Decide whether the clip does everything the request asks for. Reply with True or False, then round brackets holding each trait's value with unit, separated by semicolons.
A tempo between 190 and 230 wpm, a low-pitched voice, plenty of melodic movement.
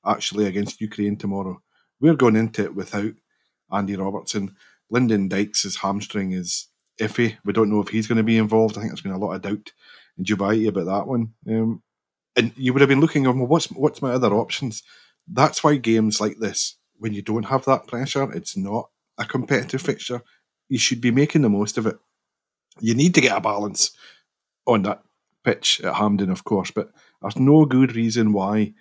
False (195 wpm; 110 Hz; 3.6 semitones)